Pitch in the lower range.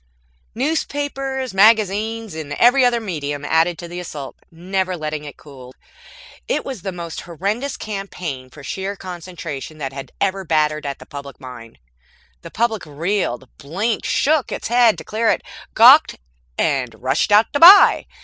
No: medium, 180 Hz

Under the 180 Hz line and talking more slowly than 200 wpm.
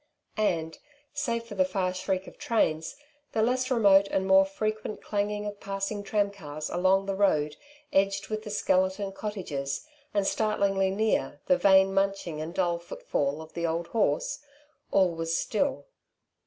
No: high, 195 Hz; average, 155 wpm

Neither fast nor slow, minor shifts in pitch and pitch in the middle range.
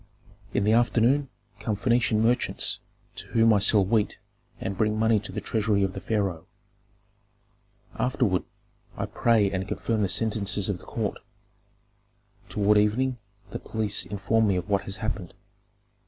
No: average, 150 wpm; narrow, 2.3 semitones; low, 105 Hz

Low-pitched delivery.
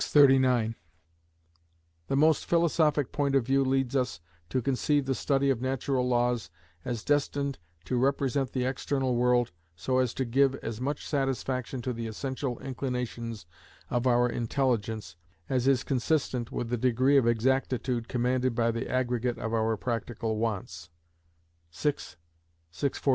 Yes: low, 125 Hz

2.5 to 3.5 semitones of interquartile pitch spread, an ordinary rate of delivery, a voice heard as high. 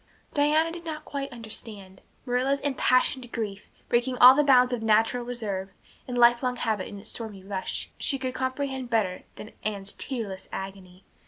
No: average, 4.3 semitones; average, 160 wpm; high, 240 Hz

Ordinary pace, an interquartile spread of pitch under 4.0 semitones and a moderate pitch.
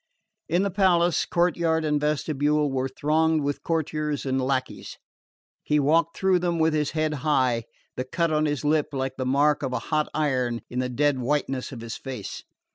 Yes: average, 185 wpm; average, 3.2 semitones; medium, 150 Hz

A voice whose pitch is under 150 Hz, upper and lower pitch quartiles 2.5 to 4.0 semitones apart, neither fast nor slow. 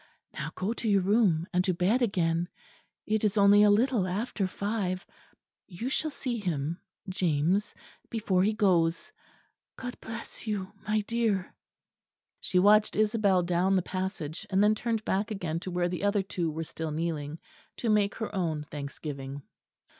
No: high, 190 Hz; average, 3.7 semitones; average, 160 wpm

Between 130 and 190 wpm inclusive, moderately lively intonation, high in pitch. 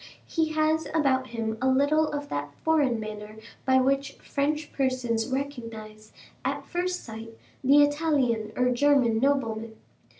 Yes: slow, 135 wpm; average, 4.4 semitones; very high, 260 Hz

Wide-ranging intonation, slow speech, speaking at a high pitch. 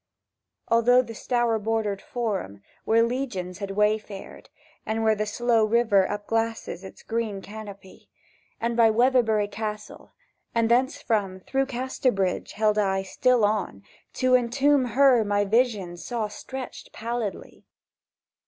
No: average, 2.8 semitones; slow, 125 wpm; high, 220 Hz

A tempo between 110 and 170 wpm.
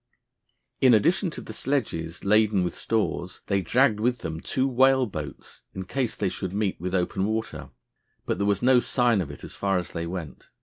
No: average, 200 wpm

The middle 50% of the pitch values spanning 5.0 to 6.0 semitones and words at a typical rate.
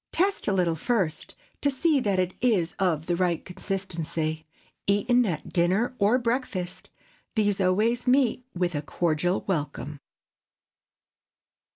No: wide, 5.5 semitones; slow, 130 wpm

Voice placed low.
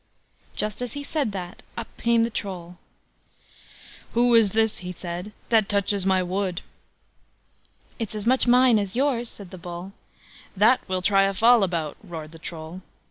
No: high, 200 Hz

